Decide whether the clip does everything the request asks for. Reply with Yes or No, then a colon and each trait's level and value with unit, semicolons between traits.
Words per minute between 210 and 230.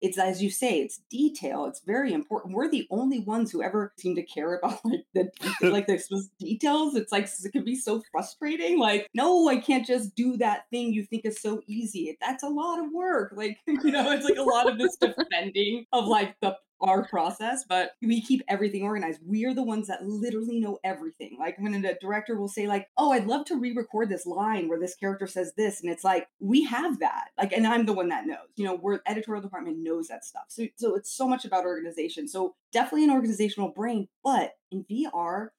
Yes: fast, 225 wpm